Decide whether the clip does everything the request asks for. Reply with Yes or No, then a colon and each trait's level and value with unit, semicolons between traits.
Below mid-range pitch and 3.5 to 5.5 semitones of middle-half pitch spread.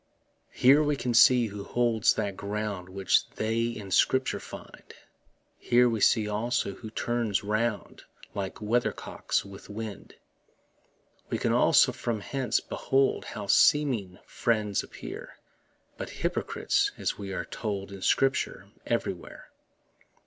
No: low, 110 Hz; average, 3.1 semitones